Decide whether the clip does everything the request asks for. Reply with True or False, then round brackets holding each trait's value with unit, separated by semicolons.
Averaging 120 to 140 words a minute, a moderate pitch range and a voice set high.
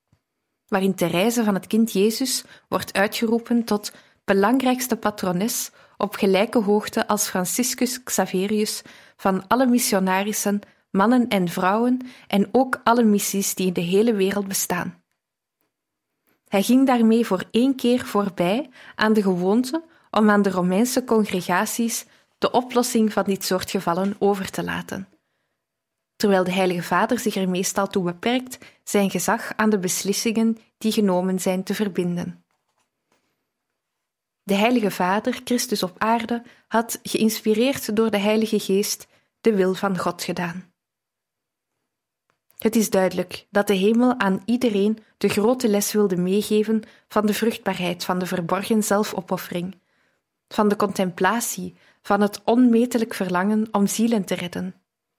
True (135 wpm; 3.2 semitones; 205 Hz)